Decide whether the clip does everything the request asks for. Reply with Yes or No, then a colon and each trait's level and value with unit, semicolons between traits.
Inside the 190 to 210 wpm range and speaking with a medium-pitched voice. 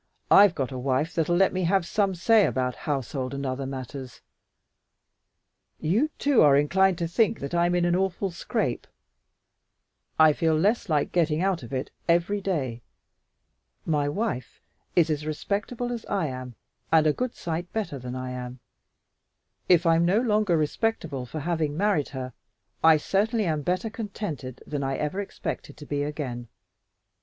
No: average, 165 wpm; medium, 160 Hz